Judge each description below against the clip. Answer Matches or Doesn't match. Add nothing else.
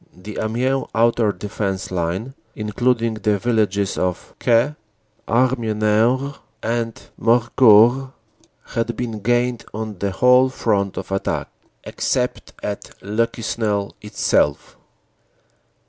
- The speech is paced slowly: Matches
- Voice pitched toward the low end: Matches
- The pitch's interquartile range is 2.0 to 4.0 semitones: Matches